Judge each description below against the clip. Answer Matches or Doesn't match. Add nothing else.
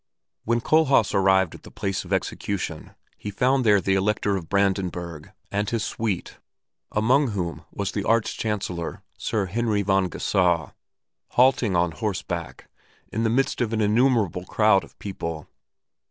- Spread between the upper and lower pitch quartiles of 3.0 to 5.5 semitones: Matches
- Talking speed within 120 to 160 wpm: Matches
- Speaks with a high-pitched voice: Doesn't match